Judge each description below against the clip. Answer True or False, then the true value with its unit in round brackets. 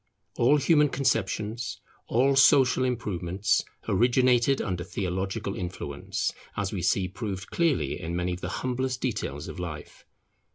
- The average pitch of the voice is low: True (105 Hz)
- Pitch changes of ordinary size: False (6.0 semitones)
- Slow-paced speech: True (130 wpm)